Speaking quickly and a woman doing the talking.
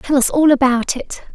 Yes: fast, 225 wpm; female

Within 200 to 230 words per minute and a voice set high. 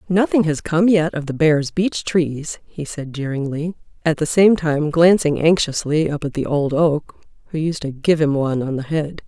No: fast, 205 wpm; medium, 155 Hz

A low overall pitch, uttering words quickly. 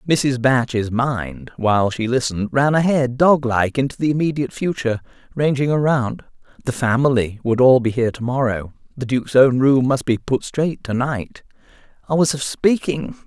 No: low, 130 Hz; average, 170 wpm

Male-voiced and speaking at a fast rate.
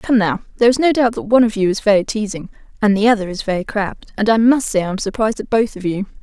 No: female; fast, 280 wpm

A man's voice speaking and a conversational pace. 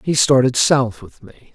Yes: male; average, 195 wpm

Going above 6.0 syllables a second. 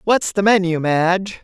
No: 4.6 syllables/s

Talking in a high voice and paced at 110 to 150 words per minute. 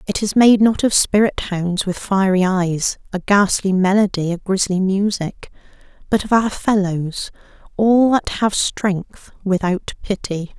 Yes: high, 195 Hz; average, 140 wpm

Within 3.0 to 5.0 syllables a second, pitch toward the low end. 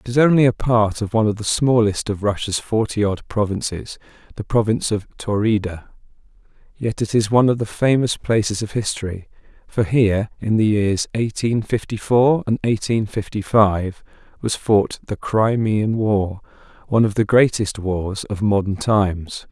Yes: 4.8 syllables/s; low, 105 Hz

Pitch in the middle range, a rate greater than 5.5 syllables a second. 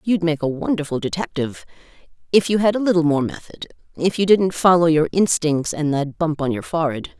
Yes: medium, 165 Hz; 5.7 syllables/s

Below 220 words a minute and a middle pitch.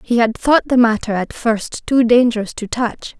No: fast, 205 wpm; high, 230 Hz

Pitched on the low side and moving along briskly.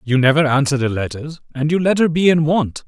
No: medium, 145 Hz; fast, 250 wpm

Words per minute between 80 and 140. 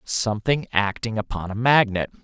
Yes: slow, 135 wpm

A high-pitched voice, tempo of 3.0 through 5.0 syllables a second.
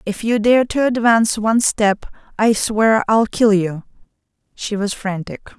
Yes: high, 215 Hz; 4.3 syllables/s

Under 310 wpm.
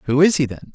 No: fast, 320 wpm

